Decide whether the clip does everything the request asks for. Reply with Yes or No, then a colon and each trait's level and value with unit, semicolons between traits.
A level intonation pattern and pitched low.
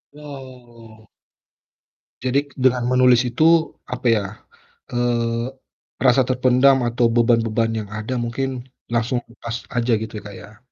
Yes: narrow, 1.7 semitones; low, 120 Hz